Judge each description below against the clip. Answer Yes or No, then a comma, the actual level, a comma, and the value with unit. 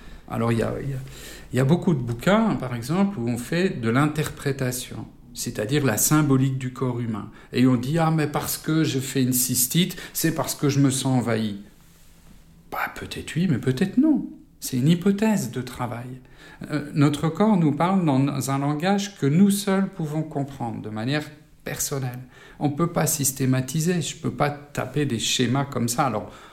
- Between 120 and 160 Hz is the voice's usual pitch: Yes, medium, 140 Hz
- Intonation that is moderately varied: Yes, average, 4.3 semitones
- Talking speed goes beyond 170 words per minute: Yes, average, 190 wpm